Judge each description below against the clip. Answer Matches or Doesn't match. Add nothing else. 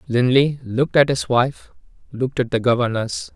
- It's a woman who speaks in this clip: Doesn't match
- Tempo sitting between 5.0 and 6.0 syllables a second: Matches